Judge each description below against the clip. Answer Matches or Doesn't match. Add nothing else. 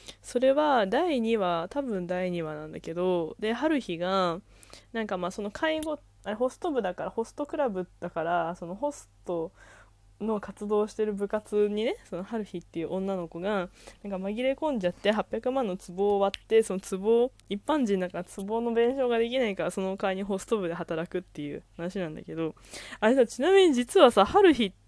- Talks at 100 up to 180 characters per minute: Doesn't match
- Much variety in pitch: Doesn't match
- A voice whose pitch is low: Doesn't match